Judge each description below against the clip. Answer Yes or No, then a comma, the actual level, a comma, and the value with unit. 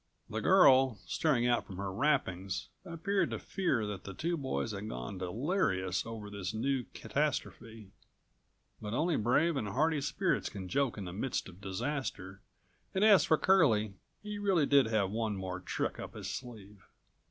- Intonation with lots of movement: Yes, wide, 7.2 semitones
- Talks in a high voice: No, low, 115 Hz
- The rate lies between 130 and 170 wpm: Yes, average, 165 wpm